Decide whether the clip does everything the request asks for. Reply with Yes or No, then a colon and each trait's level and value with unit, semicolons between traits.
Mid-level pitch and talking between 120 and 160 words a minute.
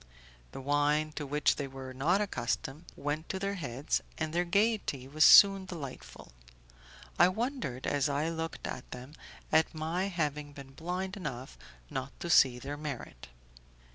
Yes: medium, 150 Hz; average, 155 wpm